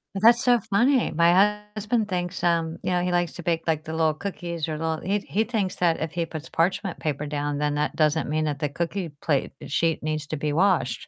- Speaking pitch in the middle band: Yes, medium, 170 Hz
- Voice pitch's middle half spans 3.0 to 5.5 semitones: Yes, average, 3.8 semitones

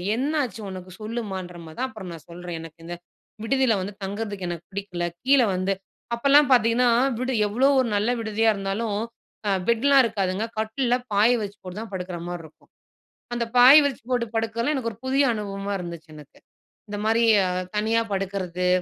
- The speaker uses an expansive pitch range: No, average, 4.2 semitones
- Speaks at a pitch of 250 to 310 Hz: No, high, 210 Hz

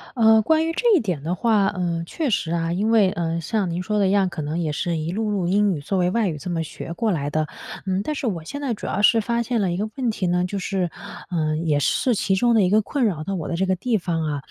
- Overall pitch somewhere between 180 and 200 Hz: Yes, high, 190 Hz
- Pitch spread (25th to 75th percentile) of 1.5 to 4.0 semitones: No, average, 4.6 semitones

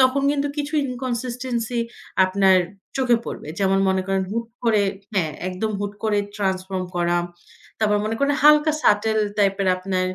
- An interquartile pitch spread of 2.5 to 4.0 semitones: No, average, 4.8 semitones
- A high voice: Yes, high, 210 Hz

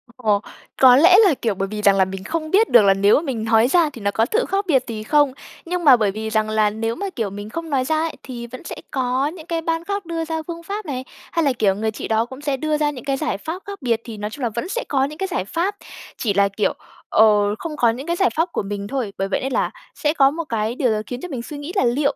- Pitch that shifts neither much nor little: No, wide, 6.7 semitones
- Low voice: No, very high, 260 Hz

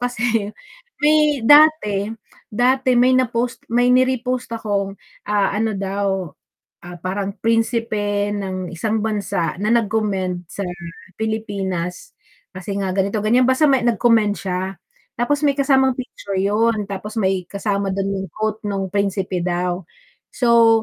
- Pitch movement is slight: No, average, 3.7 semitones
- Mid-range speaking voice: No, high, 210 Hz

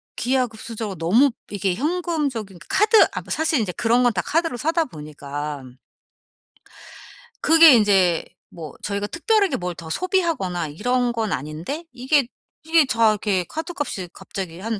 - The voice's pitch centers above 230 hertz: No, high, 225 Hz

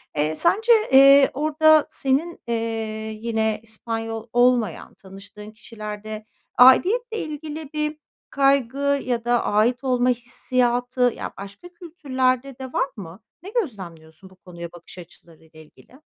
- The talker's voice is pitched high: Yes, high, 245 Hz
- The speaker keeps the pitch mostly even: No, average, 4.9 semitones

